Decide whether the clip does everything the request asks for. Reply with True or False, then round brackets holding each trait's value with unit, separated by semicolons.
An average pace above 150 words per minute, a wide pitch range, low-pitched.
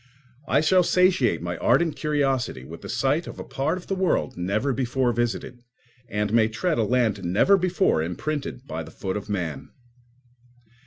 True (170 wpm; 7.4 semitones; 120 Hz)